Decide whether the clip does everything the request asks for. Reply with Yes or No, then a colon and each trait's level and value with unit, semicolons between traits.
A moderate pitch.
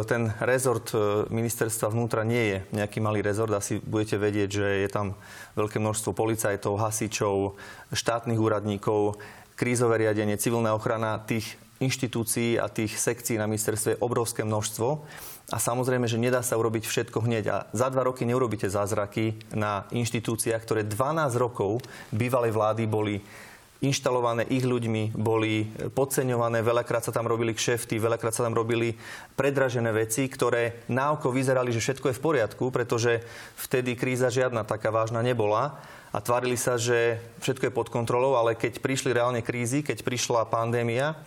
No: low, 115 Hz